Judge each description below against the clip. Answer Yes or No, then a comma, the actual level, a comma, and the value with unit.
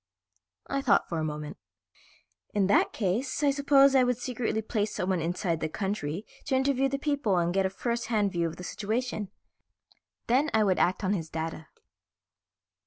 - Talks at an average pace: Yes, average, 175 wpm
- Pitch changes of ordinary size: No, wide, 6.1 semitones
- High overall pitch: Yes, high, 210 Hz